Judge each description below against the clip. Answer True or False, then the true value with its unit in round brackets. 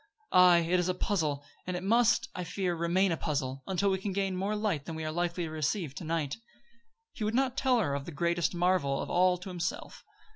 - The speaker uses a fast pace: True (230 wpm)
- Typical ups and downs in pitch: True (3.3 semitones)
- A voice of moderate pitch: True (180 Hz)